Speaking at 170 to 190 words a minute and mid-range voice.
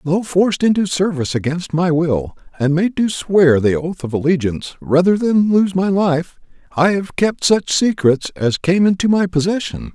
Yes: average, 180 wpm; medium, 175 Hz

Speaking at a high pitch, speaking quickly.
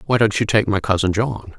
No: low, 105 Hz; fast, 265 wpm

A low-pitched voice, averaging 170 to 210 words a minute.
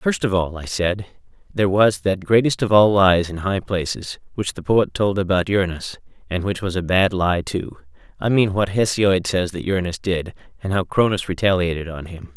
Yes: very low, 95 Hz; average, 200 wpm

